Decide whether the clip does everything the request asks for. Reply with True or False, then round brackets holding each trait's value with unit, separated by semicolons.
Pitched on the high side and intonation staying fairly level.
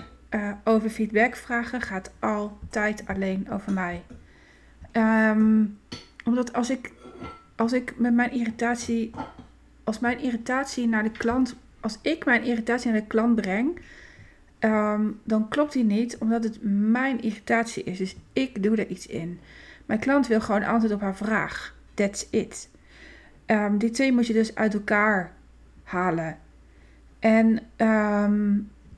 True (220 Hz; 2.3 semitones)